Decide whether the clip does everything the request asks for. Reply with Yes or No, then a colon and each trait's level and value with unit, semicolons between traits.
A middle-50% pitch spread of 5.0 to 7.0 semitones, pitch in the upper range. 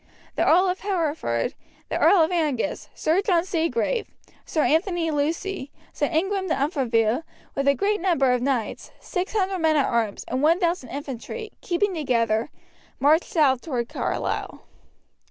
Yes: wide, 5.5 semitones; very high, 315 Hz